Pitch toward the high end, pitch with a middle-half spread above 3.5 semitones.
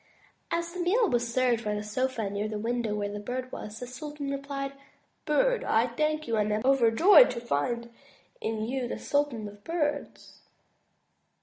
Yes: high, 245 Hz; average, 5.0 semitones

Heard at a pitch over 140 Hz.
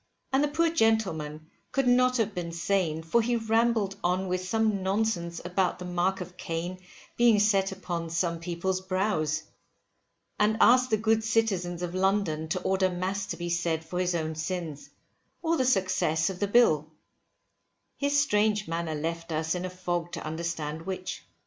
Yes: medium, 185 Hz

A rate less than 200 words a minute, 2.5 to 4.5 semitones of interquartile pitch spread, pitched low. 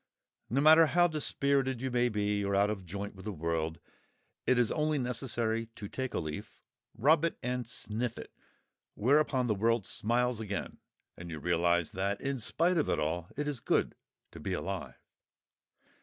No: average, 170 wpm; average, 5.2 semitones; low, 115 Hz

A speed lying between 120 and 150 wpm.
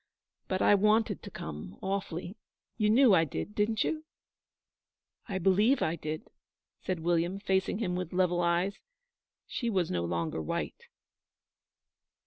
Yes: slow, 135 wpm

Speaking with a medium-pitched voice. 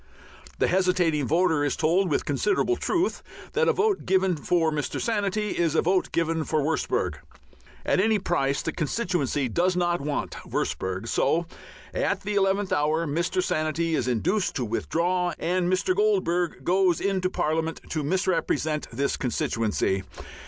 Yes: medium, 170 Hz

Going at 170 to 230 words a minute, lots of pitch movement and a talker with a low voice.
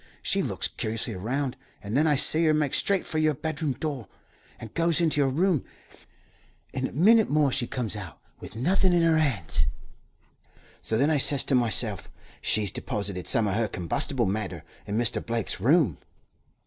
Yes: average, 175 wpm; wide, 6.2 semitones; low, 130 Hz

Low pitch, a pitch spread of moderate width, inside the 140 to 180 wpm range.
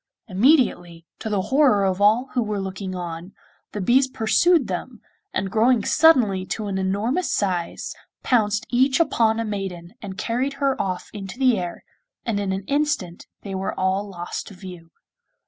No: high, 205 Hz; average, 4.7 semitones; average, 165 wpm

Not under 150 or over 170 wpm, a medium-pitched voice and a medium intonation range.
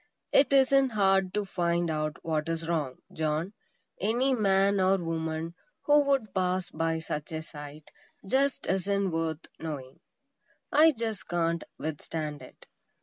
No: average, 140 wpm; medium, 175 Hz; average, 4.2 semitones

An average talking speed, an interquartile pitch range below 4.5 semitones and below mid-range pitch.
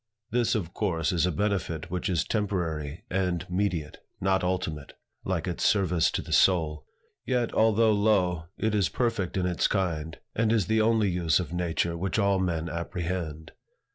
Yes: average, 170 wpm; average, 3.5 semitones; very low, 90 Hz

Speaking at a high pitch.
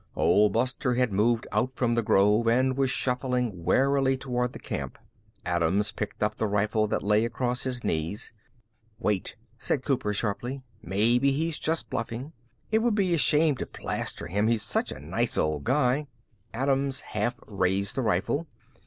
No: low, 120 Hz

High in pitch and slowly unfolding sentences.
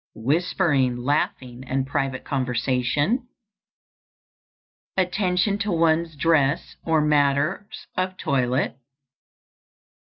No: medium, 145 Hz; slow, 85 wpm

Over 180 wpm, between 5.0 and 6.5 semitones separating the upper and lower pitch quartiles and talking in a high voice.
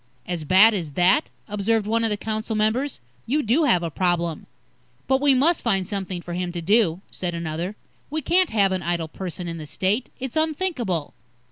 Yes: average, 195 wpm; wide, 5.4 semitones; high, 200 Hz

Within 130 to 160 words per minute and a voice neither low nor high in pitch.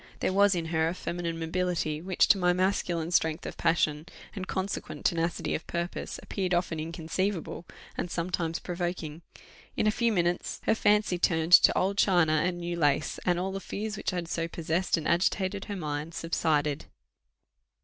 No: average, 170 wpm; medium, 175 Hz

